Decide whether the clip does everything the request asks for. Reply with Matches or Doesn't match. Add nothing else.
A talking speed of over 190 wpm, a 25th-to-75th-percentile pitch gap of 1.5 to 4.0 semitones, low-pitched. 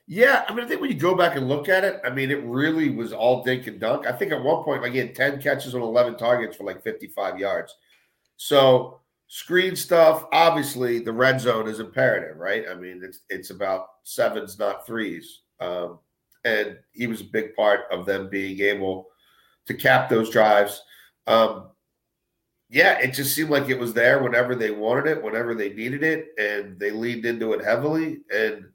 Doesn't match